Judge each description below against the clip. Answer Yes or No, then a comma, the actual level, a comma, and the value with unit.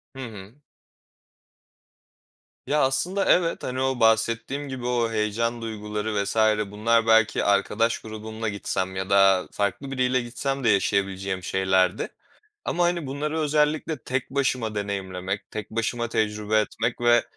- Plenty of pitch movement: No, average, 4.1 semitones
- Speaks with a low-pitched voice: Yes, low, 115 Hz